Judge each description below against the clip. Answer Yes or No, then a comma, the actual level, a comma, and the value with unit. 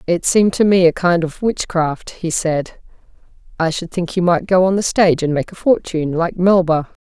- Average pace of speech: No, fast, 215 wpm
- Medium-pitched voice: Yes, medium, 175 Hz